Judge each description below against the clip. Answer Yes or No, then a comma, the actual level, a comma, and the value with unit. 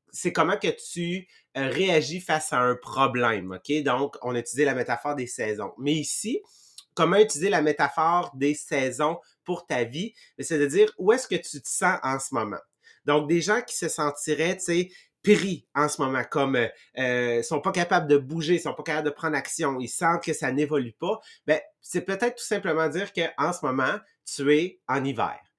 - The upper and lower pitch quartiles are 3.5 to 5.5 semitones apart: Yes, average, 4.4 semitones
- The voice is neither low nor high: Yes, medium, 155 Hz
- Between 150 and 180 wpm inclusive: No, average, 200 wpm